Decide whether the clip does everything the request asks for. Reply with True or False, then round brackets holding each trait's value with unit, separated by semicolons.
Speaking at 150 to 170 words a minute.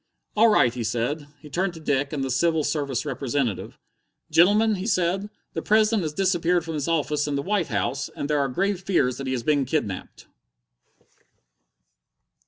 False (180 wpm)